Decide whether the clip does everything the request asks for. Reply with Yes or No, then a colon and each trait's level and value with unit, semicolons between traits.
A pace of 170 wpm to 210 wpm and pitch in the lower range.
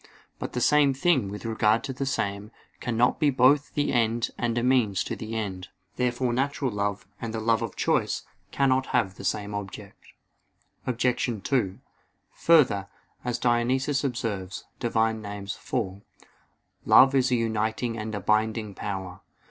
No: average, 155 wpm; low, 115 Hz